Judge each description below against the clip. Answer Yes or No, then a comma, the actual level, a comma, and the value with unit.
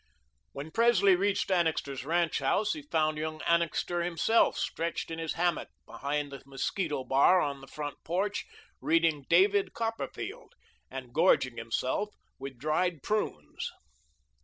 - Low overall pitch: No, medium, 165 Hz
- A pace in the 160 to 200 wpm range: No, slow, 135 wpm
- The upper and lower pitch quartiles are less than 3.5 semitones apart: No, average, 5.2 semitones